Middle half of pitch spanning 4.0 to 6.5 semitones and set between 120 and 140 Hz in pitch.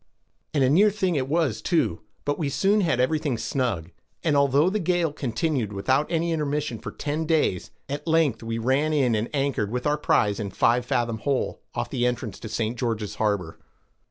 Yes: average, 5.3 semitones; low, 135 Hz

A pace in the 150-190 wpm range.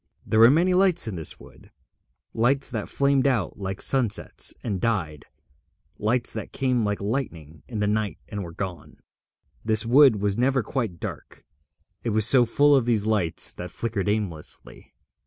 Yes: average, 165 wpm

